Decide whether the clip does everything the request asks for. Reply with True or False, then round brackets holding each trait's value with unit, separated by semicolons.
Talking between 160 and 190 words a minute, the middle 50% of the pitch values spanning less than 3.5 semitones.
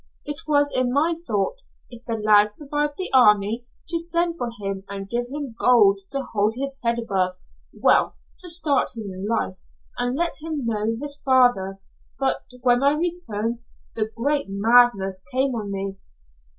False (165 wpm; 5.6 semitones)